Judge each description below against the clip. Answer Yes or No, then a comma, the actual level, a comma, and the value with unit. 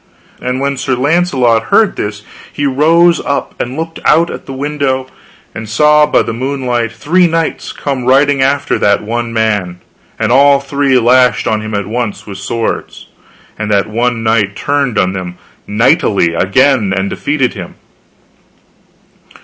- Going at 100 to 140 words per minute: No, average, 155 wpm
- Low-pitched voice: Yes, low, 125 Hz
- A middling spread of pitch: Yes, average, 4.7 semitones